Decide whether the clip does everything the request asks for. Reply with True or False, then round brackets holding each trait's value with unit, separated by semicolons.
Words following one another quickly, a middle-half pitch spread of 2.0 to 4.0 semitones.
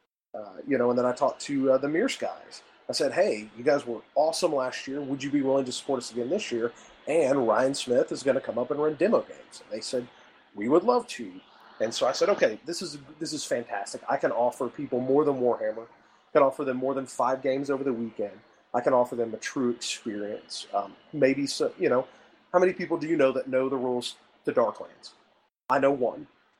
True (235 wpm; 3.3 semitones)